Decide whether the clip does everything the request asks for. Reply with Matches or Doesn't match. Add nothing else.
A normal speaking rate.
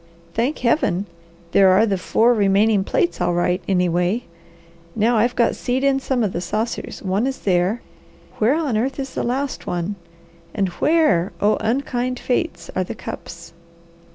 Matches